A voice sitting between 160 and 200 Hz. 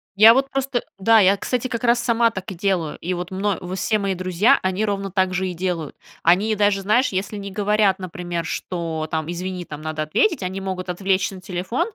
Yes: high, 190 Hz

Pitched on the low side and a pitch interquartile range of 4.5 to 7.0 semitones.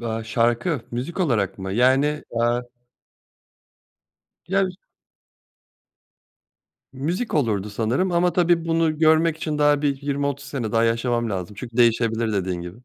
Yes: low, 125 Hz; wide, 5.6 semitones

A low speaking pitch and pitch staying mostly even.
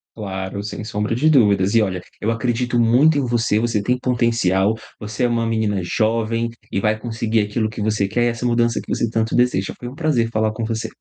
Yes: low, 115 Hz; narrow, 2.1 semitones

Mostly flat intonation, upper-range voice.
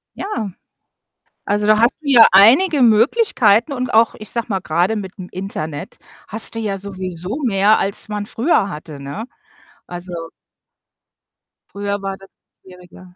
No: average, 3.4 semitones; high, 205 Hz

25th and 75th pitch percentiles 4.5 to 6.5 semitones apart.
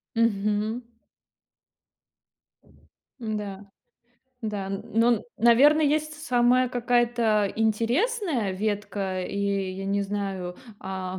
No: average, 3.6 semitones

